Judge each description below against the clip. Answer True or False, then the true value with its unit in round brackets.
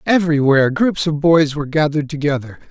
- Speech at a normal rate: True (155 wpm)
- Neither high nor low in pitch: True (150 Hz)